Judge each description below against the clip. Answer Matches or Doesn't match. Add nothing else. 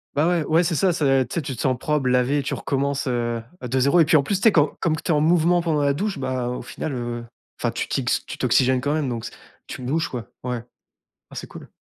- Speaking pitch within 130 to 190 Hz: Matches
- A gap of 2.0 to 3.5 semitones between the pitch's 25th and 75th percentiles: Doesn't match